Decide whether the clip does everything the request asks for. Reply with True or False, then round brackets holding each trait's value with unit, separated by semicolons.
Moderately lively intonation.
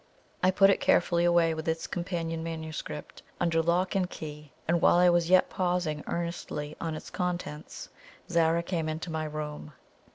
False (1.8 semitones)